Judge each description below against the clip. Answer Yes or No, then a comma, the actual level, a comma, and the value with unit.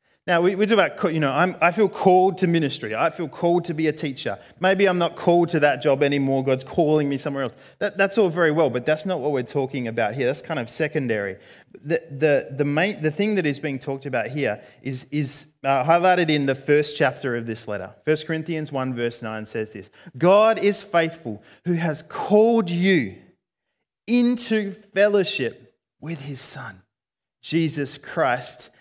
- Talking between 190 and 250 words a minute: Yes, average, 195 wpm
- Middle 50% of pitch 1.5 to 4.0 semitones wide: No, average, 5.0 semitones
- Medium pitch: Yes, medium, 155 Hz